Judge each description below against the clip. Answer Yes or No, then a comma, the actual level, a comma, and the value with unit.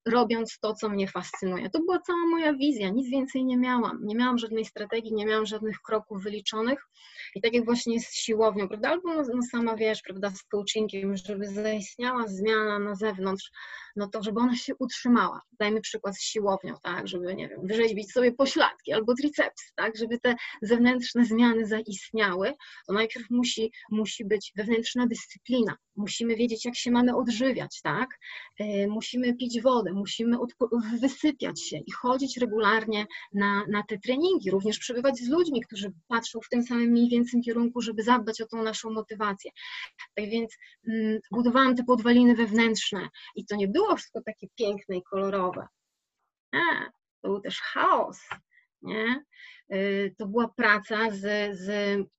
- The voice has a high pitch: Yes, high, 225 Hz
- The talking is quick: Yes, fast, 165 wpm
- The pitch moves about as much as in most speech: Yes, average, 3.0 semitones